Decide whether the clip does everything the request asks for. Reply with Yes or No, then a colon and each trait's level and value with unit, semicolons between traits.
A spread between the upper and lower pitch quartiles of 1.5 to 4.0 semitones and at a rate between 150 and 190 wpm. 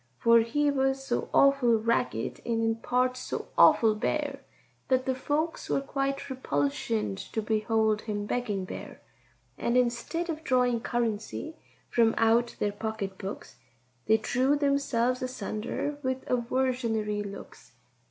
No: average, 3.3 semitones; slow, 135 wpm